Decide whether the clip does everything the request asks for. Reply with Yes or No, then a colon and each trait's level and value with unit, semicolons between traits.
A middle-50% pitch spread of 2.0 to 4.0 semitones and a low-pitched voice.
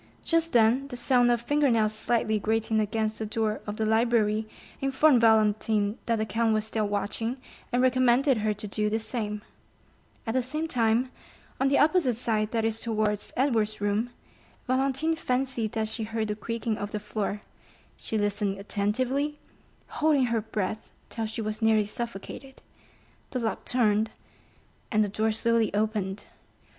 No: narrow, 2.6 semitones; high, 225 Hz